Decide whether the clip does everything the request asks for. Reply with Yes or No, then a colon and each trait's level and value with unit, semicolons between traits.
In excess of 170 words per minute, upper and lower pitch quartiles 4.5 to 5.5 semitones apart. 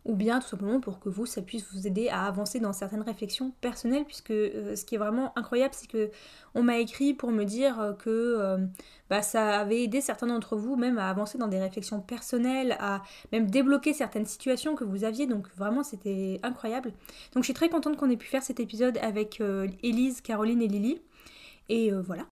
No: average, 215 wpm; average, 3.6 semitones